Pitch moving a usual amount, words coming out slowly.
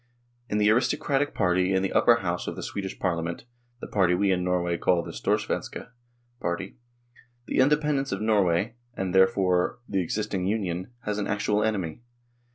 No: average, 3.3 semitones; average, 170 wpm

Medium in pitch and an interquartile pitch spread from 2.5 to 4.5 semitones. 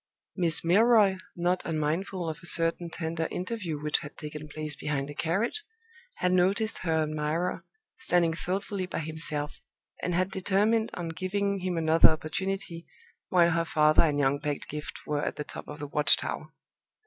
Yes: medium, 170 Hz; average, 3.4 semitones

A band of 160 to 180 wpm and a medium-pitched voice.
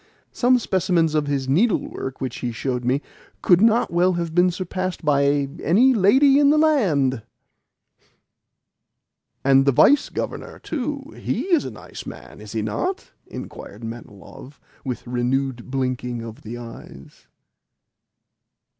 No: slow, 135 wpm; medium, 150 Hz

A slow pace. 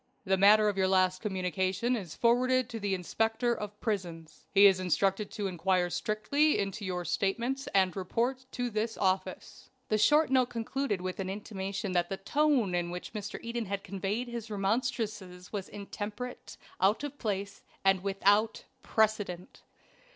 No: average, 160 wpm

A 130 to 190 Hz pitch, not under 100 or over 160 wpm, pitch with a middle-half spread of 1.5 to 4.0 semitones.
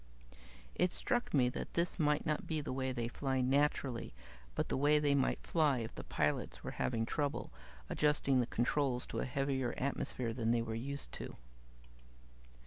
No: low, 135 Hz; average, 175 wpm; average, 3.2 semitones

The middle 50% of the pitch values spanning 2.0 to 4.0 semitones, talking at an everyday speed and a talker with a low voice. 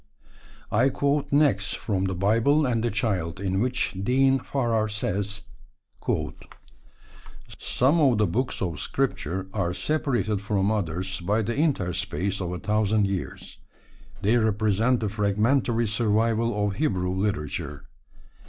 No: average, 3.7 semitones; slow, 125 wpm; low, 105 Hz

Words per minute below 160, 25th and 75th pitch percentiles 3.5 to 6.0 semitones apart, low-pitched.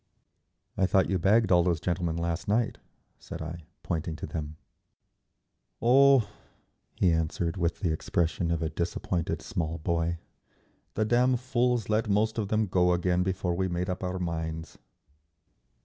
Yes: average, 150 wpm; average, 3.9 semitones; very low, 90 Hz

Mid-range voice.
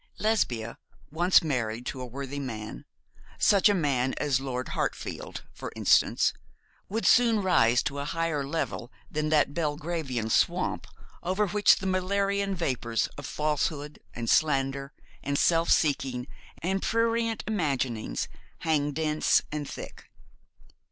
Yes: medium, 150 Hz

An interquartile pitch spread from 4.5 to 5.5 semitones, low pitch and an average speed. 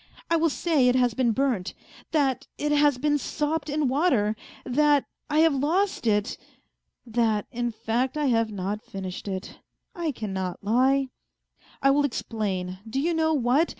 No: average, 5.2 semitones; very high, 260 Hz; average, 160 wpm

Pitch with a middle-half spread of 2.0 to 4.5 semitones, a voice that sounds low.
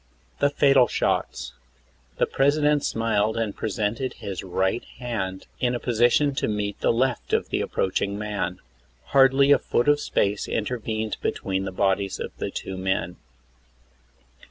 No: average, 4.9 semitones; low, 110 Hz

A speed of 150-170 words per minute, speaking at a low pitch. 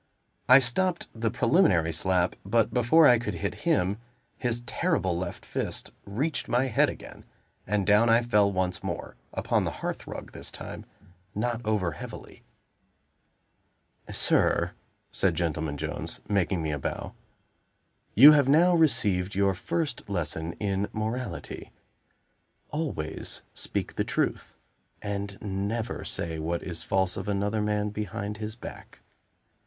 No: slow, 135 wpm; low, 105 Hz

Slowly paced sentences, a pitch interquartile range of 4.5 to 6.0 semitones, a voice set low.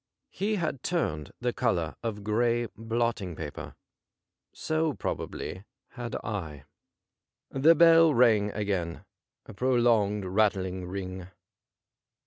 Yes: slow, 110 wpm; average, 4.9 semitones; low, 110 Hz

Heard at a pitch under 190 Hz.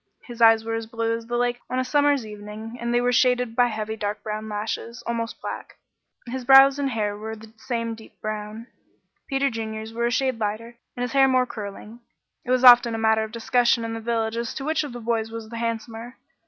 No: high, 230 Hz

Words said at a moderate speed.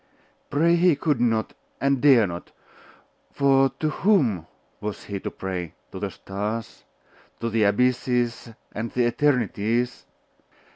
No: slow, 130 wpm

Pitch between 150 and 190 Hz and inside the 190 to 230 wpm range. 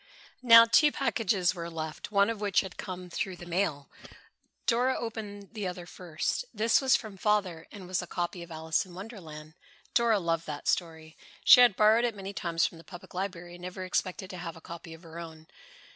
Yes: medium, 185 Hz; fast, 205 wpm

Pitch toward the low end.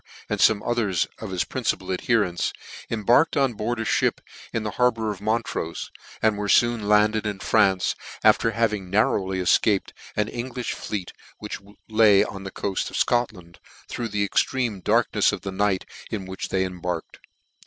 Yes: low, 105 Hz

